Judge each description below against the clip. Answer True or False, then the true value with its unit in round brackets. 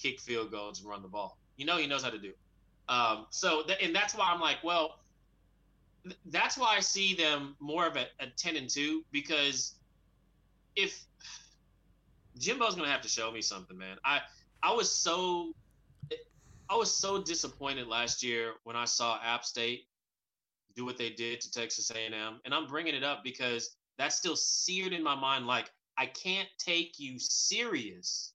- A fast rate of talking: False (185 wpm)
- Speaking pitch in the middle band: False (130 Hz)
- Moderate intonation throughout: False (6.1 semitones)